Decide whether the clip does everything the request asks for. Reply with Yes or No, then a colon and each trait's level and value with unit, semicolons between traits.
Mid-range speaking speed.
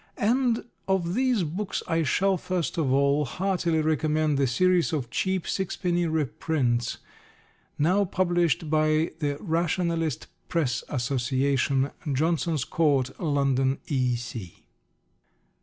No: slow, 110 wpm